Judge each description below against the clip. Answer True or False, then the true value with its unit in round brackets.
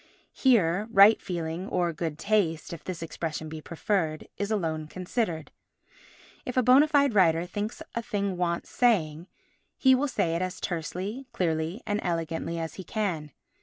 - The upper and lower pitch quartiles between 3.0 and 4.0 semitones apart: False (4.7 semitones)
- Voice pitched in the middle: True (180 Hz)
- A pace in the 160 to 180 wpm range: False (150 wpm)